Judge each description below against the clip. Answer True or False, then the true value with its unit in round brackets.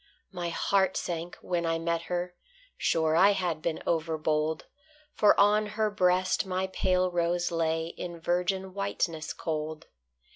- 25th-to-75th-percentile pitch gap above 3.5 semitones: False (2.5 semitones)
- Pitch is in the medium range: True (175 Hz)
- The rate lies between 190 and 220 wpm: False (140 wpm)